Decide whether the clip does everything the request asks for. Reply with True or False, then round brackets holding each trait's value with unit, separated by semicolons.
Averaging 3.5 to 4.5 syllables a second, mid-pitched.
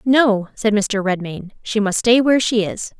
False (4.4 syllables/s; 215 Hz)